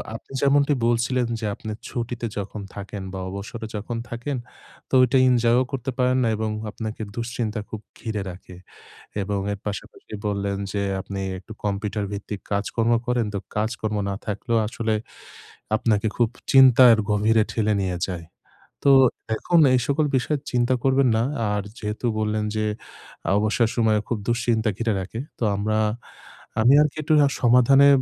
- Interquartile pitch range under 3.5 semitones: Yes, average, 2.9 semitones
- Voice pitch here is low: Yes, low, 115 Hz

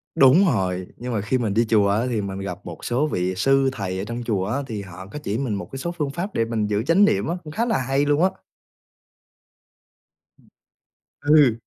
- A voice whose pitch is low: Yes, low, 115 Hz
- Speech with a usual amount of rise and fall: No, wide, 6.0 semitones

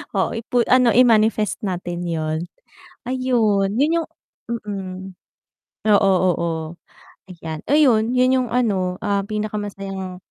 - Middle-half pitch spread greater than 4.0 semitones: Yes, average, 4.6 semitones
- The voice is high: Yes, high, 210 Hz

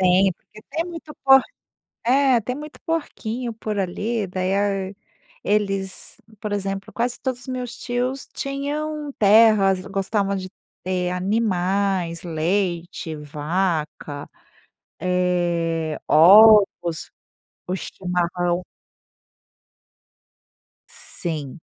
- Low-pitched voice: No, high, 195 Hz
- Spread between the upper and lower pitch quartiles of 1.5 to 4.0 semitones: No, average, 4.6 semitones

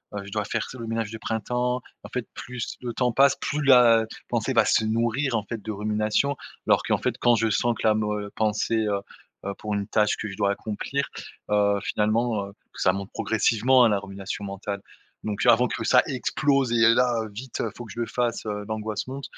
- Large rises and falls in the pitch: No, average, 2.8 semitones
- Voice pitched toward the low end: Yes, low, 110 Hz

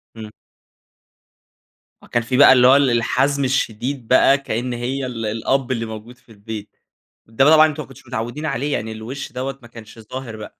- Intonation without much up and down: No, average, 3.3 semitones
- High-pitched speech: No, low, 125 Hz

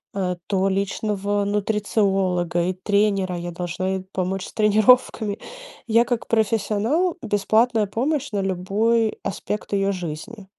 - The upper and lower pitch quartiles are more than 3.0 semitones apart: No, average, 2.7 semitones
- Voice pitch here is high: Yes, high, 200 Hz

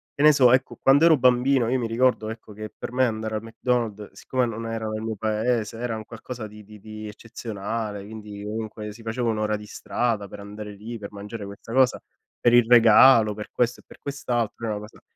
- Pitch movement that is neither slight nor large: No, narrow, 2.3 semitones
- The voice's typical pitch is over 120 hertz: No, low, 110 Hz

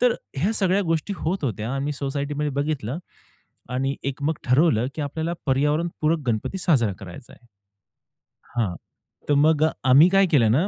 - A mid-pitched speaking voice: Yes, medium, 145 Hz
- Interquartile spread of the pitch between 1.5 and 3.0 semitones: No, average, 3.8 semitones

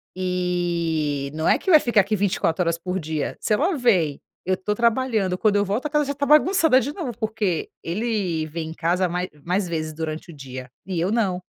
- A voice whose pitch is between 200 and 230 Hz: No, medium, 185 Hz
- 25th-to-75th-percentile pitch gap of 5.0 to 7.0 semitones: Yes, wide, 5.5 semitones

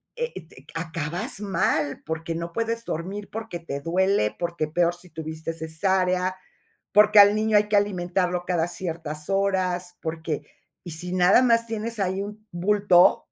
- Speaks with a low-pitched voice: No, medium, 180 Hz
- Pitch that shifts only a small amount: No, average, 3.5 semitones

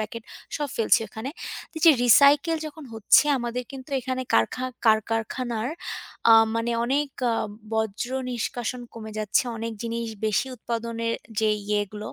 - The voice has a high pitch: Yes, high, 230 Hz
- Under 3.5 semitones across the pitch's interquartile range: Yes, average, 2.8 semitones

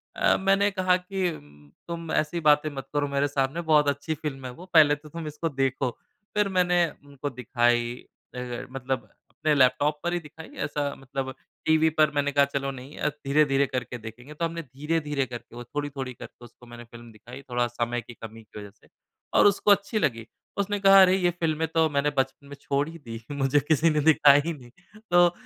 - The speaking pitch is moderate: Yes, medium, 145 Hz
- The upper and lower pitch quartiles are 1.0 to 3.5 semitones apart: No, average, 4.2 semitones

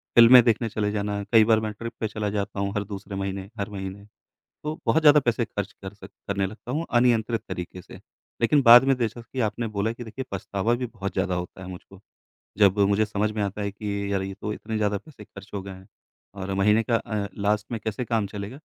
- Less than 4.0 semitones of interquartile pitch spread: Yes, narrow, 2.6 semitones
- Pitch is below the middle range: Yes, low, 105 Hz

